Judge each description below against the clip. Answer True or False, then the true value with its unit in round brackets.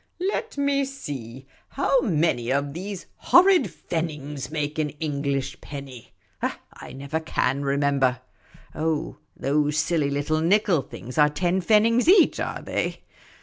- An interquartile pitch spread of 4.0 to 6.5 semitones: True (5.2 semitones)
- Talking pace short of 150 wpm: True (135 wpm)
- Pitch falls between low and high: True (150 Hz)